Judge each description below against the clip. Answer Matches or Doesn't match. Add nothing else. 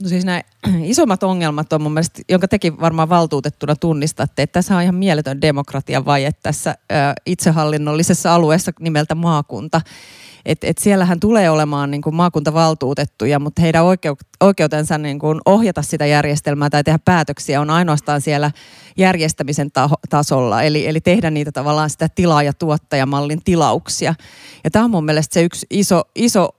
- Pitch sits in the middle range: Matches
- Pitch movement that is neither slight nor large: Matches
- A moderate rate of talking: Doesn't match